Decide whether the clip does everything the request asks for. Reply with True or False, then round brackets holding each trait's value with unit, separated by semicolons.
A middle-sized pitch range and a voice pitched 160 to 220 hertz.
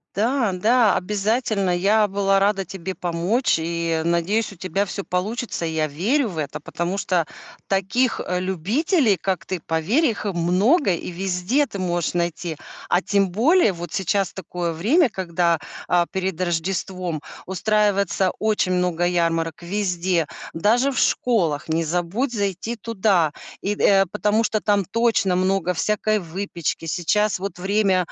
True (3.5 semitones; 190 Hz)